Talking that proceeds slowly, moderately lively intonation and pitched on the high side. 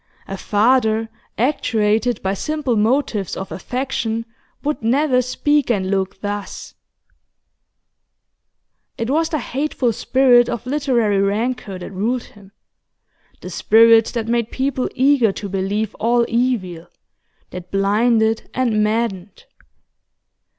Yes: slow, 115 wpm; average, 3.7 semitones; high, 230 Hz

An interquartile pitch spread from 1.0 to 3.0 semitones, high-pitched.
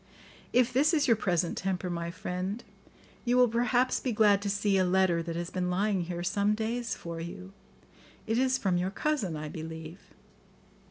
No: average, 4.9 semitones; high, 195 Hz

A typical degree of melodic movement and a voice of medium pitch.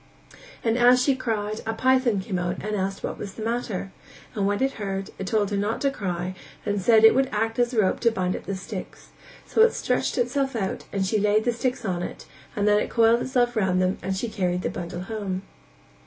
No: average, 3.7 semitones; high, 210 Hz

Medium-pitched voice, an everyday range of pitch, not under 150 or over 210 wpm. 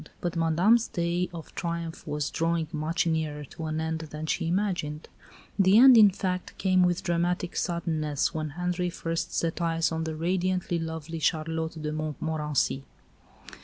No: medium, 165 Hz; narrow, 2.1 semitones; average, 155 wpm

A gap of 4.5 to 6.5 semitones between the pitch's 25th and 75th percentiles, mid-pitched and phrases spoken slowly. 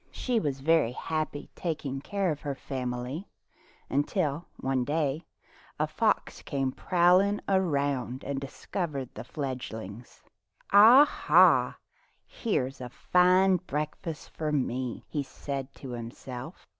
Yes: average, 5.0 semitones; medium, 145 Hz; slow, 120 wpm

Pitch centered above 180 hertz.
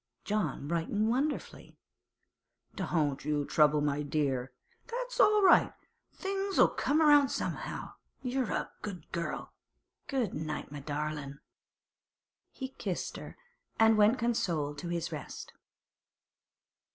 No: medium, 170 Hz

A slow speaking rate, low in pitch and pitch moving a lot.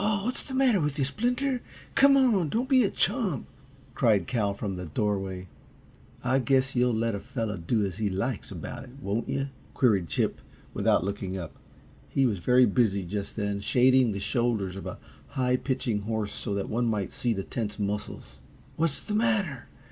No: average, 185 wpm; low, 120 Hz; wide, 5.8 semitones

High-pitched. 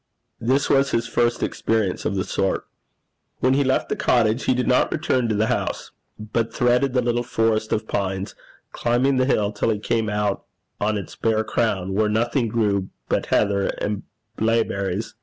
No: low, 110 Hz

